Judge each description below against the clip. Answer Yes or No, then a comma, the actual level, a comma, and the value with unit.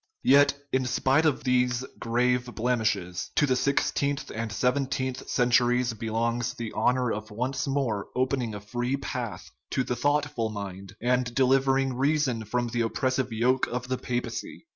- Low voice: Yes, low, 125 Hz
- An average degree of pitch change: No, narrow, 2.3 semitones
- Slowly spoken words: No, average, 155 wpm